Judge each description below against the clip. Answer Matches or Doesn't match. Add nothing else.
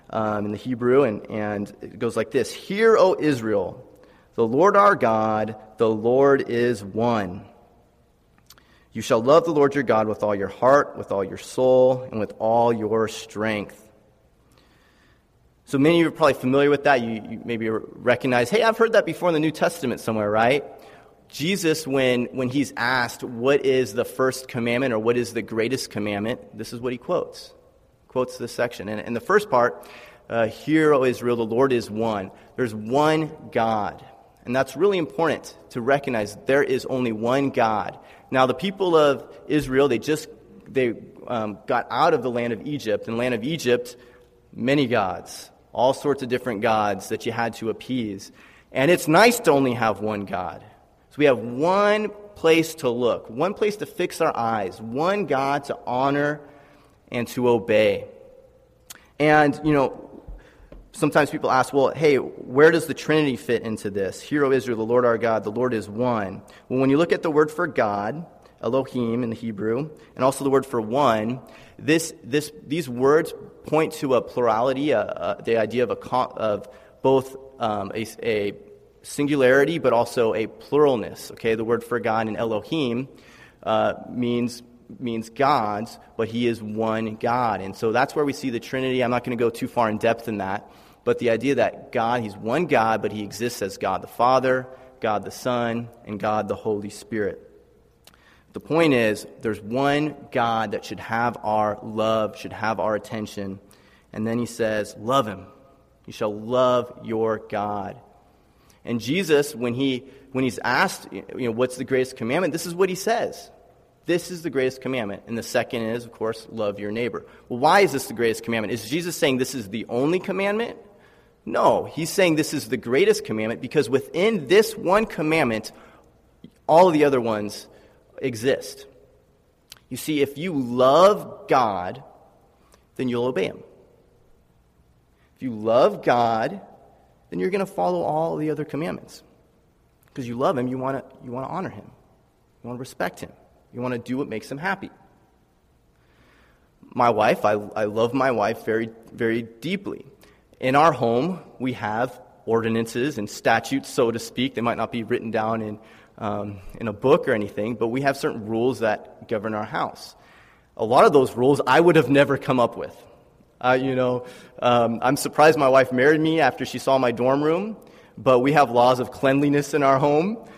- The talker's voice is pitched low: Matches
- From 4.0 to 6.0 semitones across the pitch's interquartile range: Matches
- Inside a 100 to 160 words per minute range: Doesn't match